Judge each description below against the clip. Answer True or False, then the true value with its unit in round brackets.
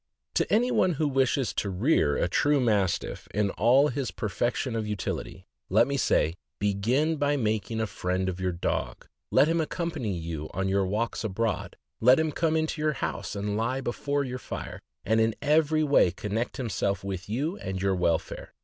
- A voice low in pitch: True (115 Hz)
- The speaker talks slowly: False (185 wpm)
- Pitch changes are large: True (6.5 semitones)